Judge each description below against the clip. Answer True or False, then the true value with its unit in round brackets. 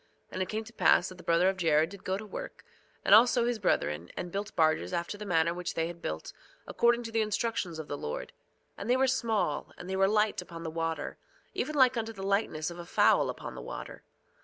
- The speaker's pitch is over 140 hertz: True (190 Hz)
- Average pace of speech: False (235 wpm)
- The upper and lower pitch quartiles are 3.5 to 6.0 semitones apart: True (4.9 semitones)